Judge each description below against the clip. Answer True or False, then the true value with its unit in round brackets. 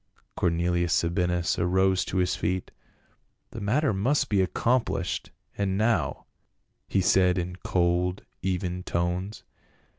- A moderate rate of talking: False (115 wpm)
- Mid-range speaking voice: False (90 Hz)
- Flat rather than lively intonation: True (2.1 semitones)